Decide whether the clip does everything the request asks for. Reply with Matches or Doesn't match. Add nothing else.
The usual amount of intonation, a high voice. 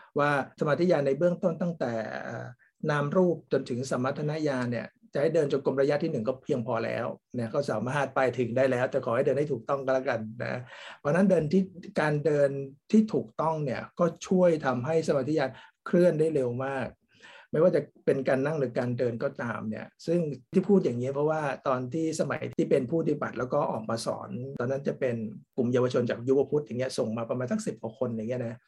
Doesn't match